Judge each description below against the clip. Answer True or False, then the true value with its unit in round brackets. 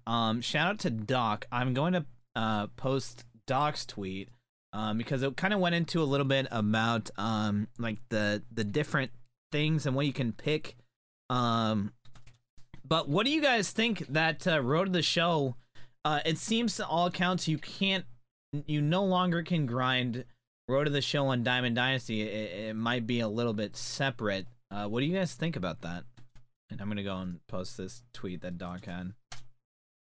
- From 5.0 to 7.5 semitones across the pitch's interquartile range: True (5.4 semitones)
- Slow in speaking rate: False (190 wpm)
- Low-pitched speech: True (125 Hz)